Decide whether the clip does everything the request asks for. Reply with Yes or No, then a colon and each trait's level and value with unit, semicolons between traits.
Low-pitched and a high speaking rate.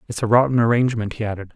Yes: low, 115 Hz; fast, 230 wpm